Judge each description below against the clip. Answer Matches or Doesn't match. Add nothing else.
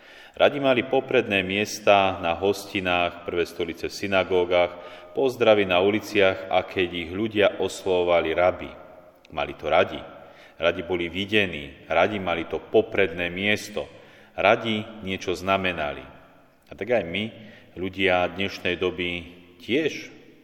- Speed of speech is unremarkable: Matches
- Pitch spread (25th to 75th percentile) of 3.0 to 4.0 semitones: Doesn't match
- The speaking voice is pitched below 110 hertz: Matches